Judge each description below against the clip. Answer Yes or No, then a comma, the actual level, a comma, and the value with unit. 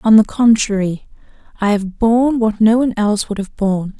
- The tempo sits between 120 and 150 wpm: No, average, 195 wpm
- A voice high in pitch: Yes, high, 215 Hz